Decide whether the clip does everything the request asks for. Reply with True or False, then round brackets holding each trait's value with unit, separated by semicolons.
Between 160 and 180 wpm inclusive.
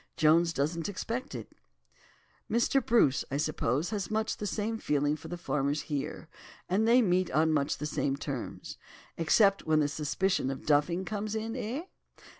True (165 wpm)